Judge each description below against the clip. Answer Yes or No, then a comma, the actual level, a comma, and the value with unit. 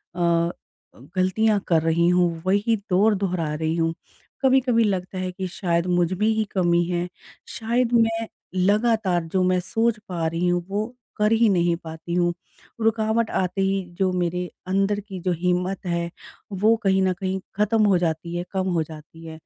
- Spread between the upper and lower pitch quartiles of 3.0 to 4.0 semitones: Yes, average, 3.4 semitones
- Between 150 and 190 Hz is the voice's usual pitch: Yes, medium, 185 Hz